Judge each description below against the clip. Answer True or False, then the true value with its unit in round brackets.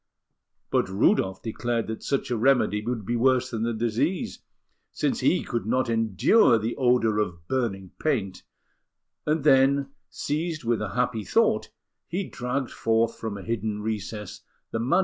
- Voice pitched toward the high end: False (115 Hz)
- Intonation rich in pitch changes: False (3.5 semitones)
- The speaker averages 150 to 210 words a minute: True (155 wpm)